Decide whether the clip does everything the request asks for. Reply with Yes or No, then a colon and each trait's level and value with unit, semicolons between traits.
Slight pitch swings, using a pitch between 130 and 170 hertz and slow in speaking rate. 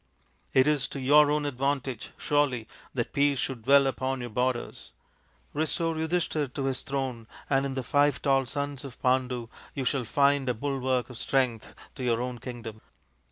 No: narrow, 2.3 semitones; low, 135 Hz; average, 170 wpm